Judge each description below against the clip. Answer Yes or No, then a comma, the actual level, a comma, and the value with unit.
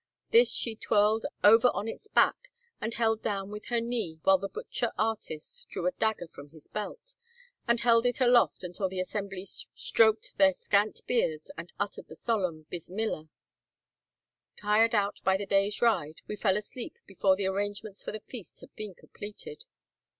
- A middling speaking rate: Yes, average, 170 wpm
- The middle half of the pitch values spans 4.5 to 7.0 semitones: No, average, 3.1 semitones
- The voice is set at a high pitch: Yes, high, 210 Hz